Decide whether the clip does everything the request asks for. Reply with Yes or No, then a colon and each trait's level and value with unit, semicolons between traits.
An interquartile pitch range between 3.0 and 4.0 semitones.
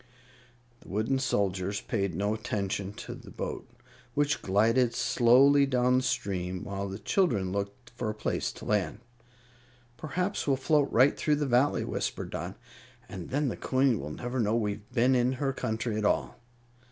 No: average, 4.5 semitones